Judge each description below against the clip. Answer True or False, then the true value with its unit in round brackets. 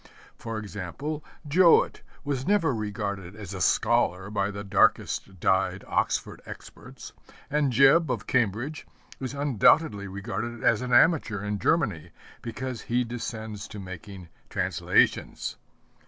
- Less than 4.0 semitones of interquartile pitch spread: False (4.8 semitones)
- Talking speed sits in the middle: False (125 wpm)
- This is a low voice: True (110 Hz)